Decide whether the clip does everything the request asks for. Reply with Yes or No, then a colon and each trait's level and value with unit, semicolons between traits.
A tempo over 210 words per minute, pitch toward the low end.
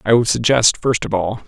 Yes: fast, 245 wpm; low, 115 Hz